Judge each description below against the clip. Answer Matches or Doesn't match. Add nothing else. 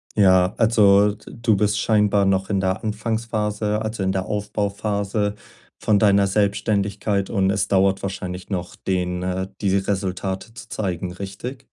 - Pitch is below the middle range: Matches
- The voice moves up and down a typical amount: Doesn't match